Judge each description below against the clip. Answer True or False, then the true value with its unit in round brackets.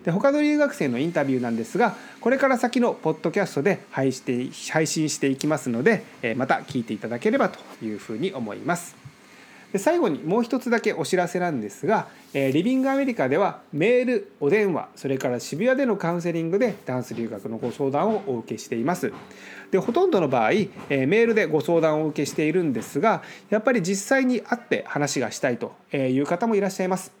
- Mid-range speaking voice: True (180 Hz)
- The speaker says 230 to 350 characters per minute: False (410 characters per minute)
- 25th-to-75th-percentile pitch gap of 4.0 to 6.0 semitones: False (8.7 semitones)